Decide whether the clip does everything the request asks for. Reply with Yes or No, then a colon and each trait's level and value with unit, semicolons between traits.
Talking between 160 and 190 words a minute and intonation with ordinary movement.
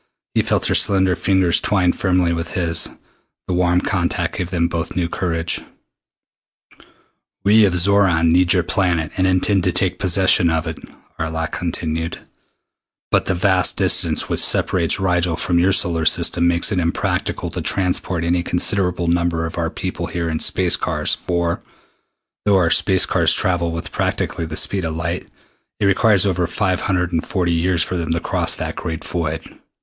No: average, 170 wpm; narrow, 1.8 semitones